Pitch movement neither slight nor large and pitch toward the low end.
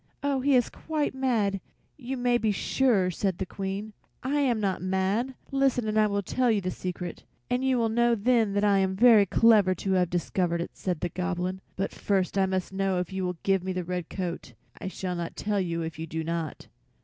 No: average, 4.3 semitones; high, 195 Hz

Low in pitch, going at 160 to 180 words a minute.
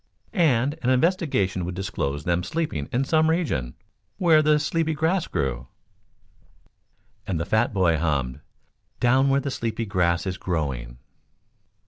No: low, 110 Hz; slow, 135 wpm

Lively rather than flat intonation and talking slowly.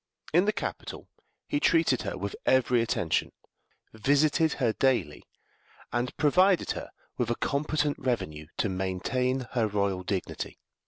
Yes: wide, 6.7 semitones; slow, 130 wpm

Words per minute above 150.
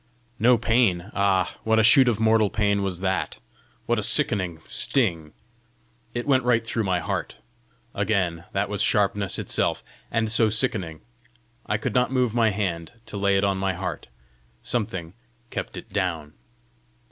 Yes: average, 160 wpm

